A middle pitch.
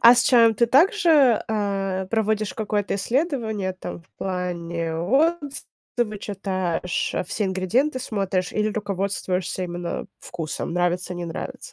No: high, 200 Hz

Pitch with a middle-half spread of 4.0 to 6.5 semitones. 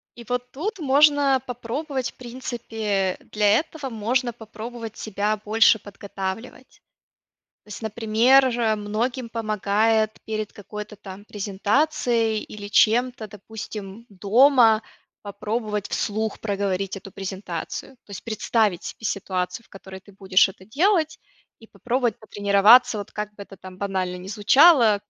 No: average, 3.2 semitones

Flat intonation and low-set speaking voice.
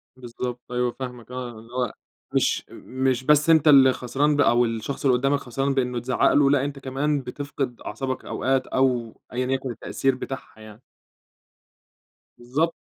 Yes: narrow, 2.0 semitones; low, 130 Hz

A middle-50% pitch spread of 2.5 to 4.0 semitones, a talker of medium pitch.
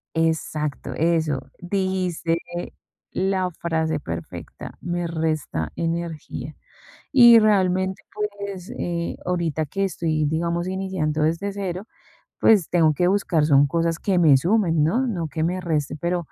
Yes: average, 2.9 semitones; medium, 170 Hz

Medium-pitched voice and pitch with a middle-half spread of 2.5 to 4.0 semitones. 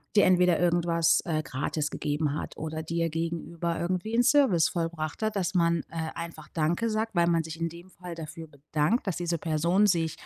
No: medium, 170 Hz; narrow, 2.0 semitones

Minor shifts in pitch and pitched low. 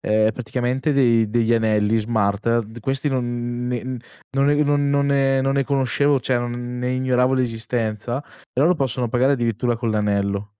No: average, 3.0 semitones; low, 120 Hz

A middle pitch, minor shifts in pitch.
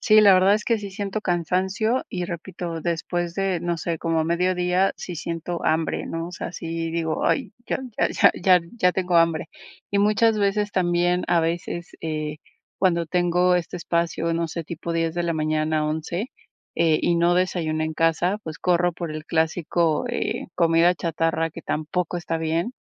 Yes: medium, 170 Hz; narrow, 1.8 semitones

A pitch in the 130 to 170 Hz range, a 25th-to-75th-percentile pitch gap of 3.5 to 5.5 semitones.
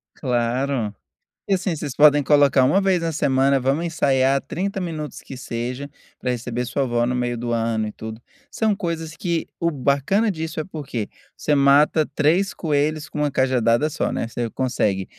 Yes: medium, 140 Hz; average, 4.4 semitones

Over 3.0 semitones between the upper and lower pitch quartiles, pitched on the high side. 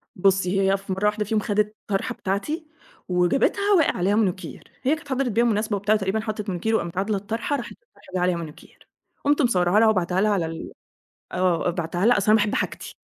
Yes: average, 3.4 semitones; high, 205 Hz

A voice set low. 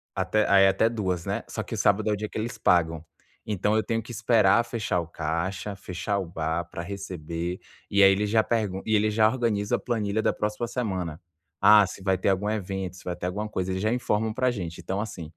Yes: low, 100 Hz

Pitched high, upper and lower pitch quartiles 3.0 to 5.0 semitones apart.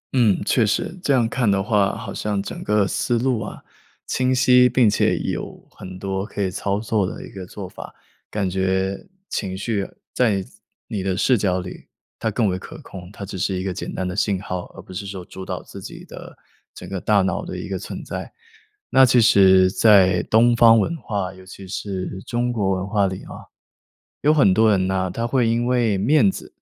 No: low, 100 Hz; average, 3.5 semitones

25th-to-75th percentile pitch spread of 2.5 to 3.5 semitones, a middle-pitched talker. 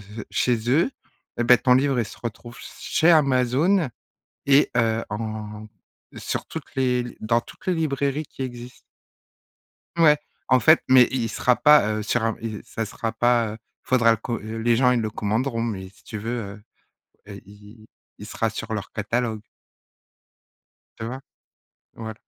No: average, 2.9 semitones; low, 120 Hz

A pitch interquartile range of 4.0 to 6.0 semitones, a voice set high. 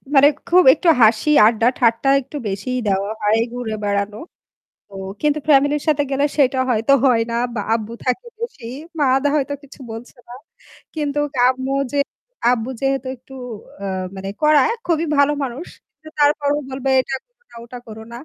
Yes: average, 4.3 semitones; very high, 265 Hz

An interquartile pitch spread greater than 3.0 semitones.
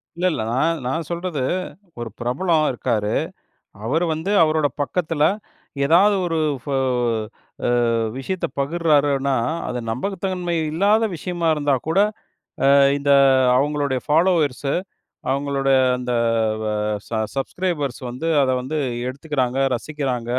Yes: average, 4.1 semitones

